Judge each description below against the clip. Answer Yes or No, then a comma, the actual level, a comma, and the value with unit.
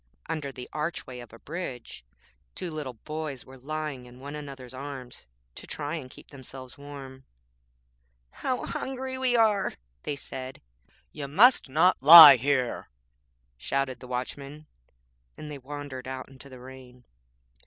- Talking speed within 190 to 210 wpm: No, average, 145 wpm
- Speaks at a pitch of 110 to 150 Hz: Yes, medium, 140 Hz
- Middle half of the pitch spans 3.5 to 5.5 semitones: No, average, 3.0 semitones